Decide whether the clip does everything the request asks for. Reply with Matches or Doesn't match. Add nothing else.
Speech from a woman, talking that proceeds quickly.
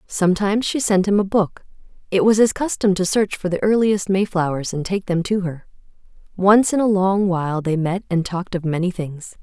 Matches